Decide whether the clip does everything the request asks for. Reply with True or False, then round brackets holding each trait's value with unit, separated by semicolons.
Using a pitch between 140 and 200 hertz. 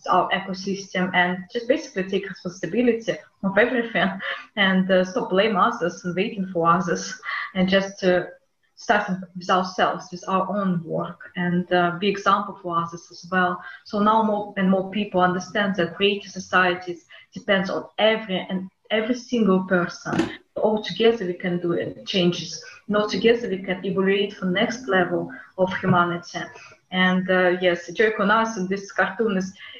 True (190 Hz)